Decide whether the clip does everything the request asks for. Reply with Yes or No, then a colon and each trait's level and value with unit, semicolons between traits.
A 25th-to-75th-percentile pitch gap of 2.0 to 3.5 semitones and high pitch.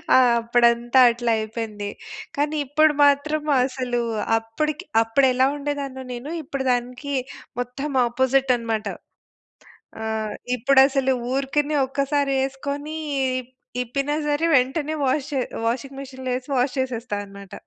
Yes: average, 2.9 semitones; very high, 260 Hz